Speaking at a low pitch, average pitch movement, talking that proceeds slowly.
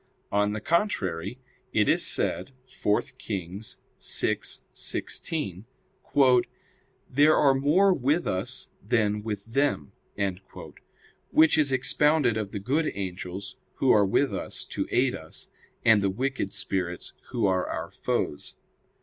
No: low, 110 Hz; wide, 5.9 semitones; slow, 125 wpm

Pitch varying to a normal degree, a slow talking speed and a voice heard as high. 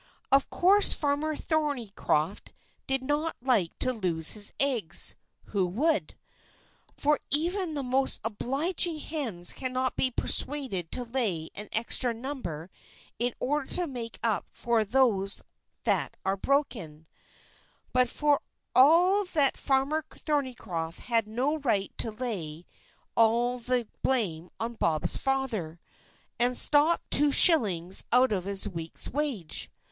No: wide, 6.2 semitones; slow, 125 wpm; very high, 250 Hz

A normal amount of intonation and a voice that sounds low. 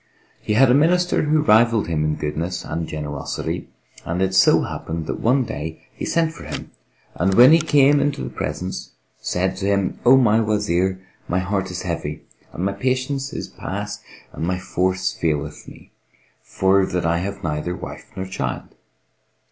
No: wide, 6.4 semitones; very low, 95 Hz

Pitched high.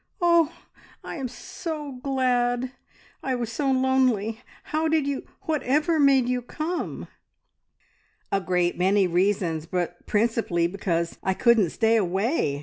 Yes: high, 240 Hz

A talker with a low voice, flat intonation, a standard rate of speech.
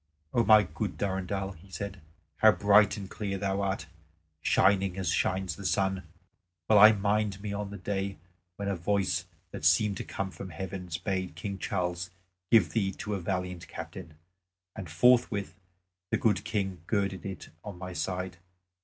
Yes: very low, 95 Hz; narrow, 1.8 semitones; average, 165 wpm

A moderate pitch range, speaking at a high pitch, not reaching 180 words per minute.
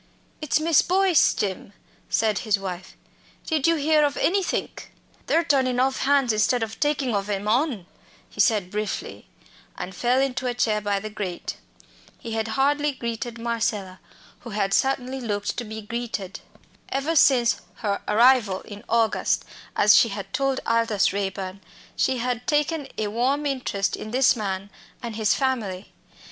Yes: average, 4.5 semitones; high, 235 Hz; average, 155 wpm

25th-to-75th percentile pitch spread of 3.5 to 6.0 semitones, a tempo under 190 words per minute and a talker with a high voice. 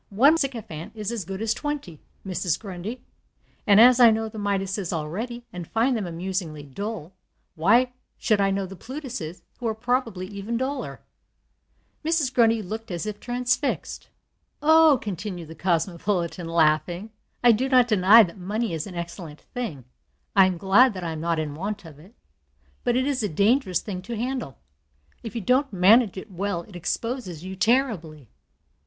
Yes: average, 5.3 semitones; average, 170 wpm; high, 200 Hz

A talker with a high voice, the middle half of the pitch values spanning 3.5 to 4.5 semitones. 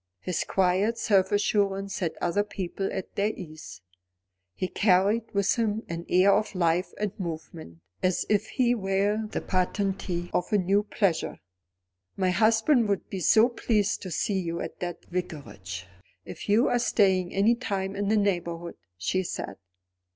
No: high, 195 Hz; average, 2.9 semitones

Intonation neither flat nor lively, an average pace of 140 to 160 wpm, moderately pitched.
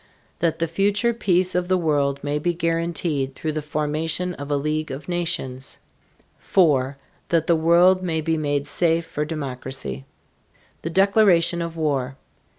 Yes: average, 3.2 semitones; average, 155 wpm; medium, 160 Hz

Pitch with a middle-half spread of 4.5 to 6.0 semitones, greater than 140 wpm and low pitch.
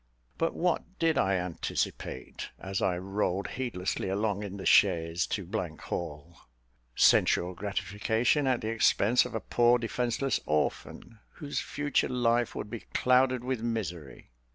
No: average, 5.1 semitones; slow, 135 wpm; low, 110 Hz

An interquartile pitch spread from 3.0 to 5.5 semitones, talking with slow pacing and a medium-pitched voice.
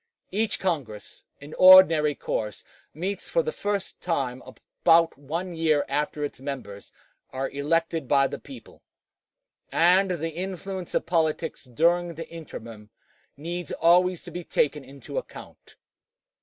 Yes: average, 4.1 semitones; slow, 130 wpm; medium, 165 Hz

